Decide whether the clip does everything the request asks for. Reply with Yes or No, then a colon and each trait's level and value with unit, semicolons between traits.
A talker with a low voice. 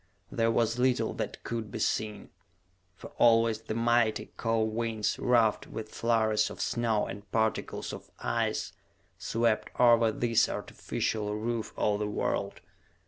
Yes: low, 115 Hz